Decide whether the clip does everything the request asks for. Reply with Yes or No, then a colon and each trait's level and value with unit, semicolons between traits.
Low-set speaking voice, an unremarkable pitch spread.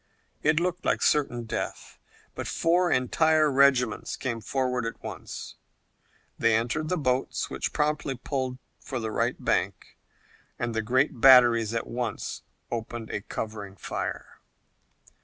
Yes: low, 125 Hz; average, 4.2 semitones